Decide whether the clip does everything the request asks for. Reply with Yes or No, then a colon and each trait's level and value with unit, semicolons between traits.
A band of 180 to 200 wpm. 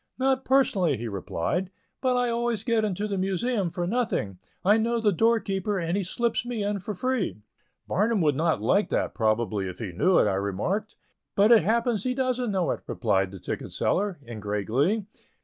Yes: average, 190 wpm